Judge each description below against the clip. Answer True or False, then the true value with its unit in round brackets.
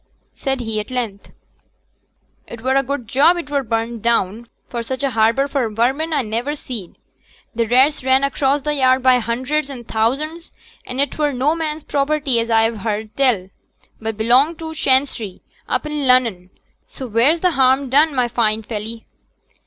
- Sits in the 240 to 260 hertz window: True (255 Hz)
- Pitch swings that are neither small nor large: True (3.7 semitones)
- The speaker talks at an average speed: True (175 wpm)